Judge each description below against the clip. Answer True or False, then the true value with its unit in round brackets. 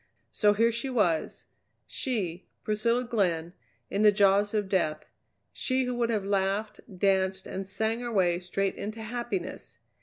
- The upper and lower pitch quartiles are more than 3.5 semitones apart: False (3.2 semitones)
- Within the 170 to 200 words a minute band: False (150 wpm)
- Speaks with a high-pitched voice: True (205 Hz)